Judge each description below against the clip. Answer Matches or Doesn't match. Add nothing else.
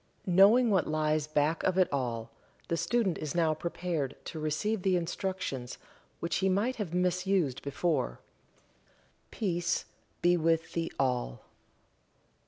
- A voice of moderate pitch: Matches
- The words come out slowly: Matches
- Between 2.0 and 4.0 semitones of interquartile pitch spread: Matches